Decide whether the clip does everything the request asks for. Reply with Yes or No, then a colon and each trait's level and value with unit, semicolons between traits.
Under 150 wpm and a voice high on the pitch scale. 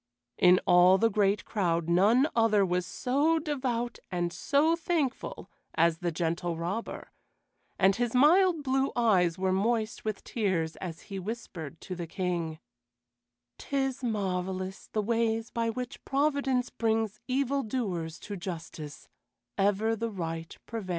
Yes: slow, 135 wpm; high, 210 Hz